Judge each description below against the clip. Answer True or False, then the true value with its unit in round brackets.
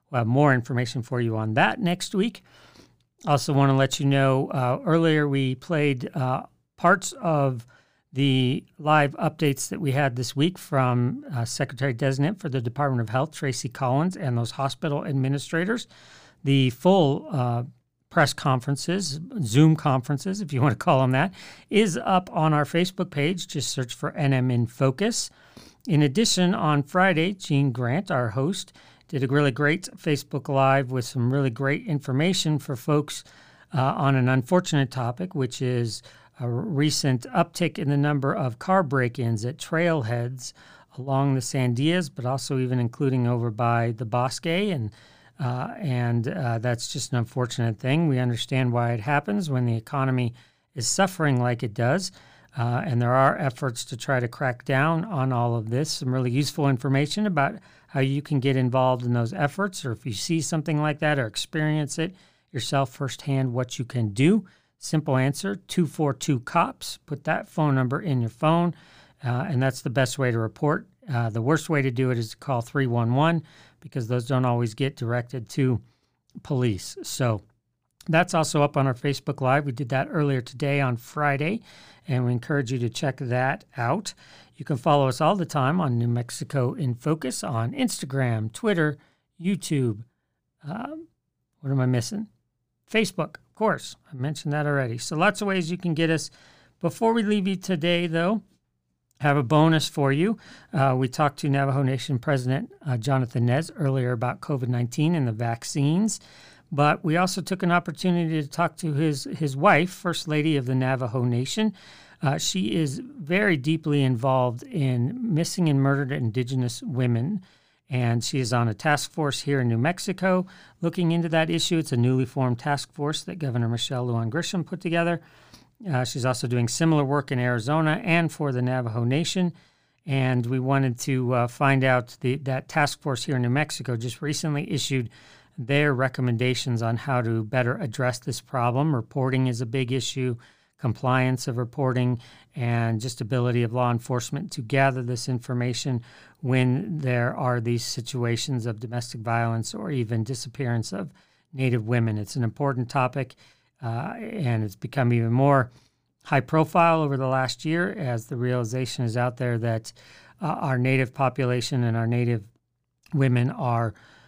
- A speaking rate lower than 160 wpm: False (175 wpm)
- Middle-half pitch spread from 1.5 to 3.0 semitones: False (3.9 semitones)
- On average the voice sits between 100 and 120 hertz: False (135 Hz)